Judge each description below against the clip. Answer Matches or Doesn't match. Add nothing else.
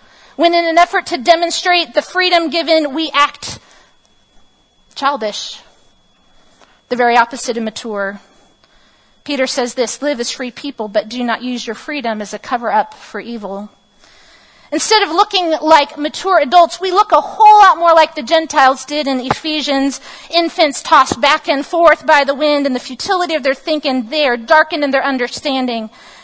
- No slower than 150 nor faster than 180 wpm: Matches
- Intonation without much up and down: Doesn't match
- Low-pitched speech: Doesn't match